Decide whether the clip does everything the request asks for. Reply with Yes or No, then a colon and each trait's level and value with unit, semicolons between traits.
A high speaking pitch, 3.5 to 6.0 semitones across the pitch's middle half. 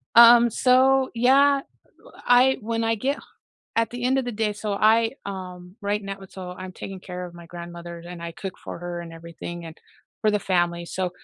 Yes: high, 200 Hz; average, 5.3 semitones